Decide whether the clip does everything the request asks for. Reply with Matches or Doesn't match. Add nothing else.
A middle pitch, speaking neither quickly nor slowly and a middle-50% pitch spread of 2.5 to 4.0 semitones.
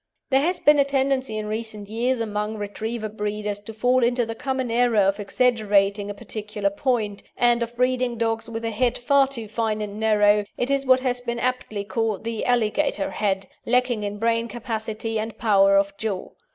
Doesn't match